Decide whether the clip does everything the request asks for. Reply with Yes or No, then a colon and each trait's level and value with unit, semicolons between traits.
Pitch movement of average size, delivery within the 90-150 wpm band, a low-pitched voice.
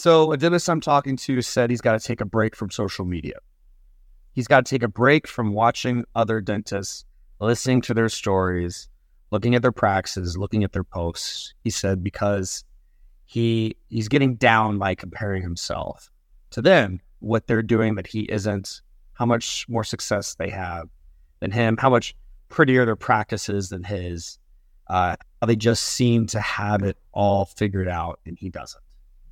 No: average, 4.5 semitones; average, 175 wpm; low, 105 Hz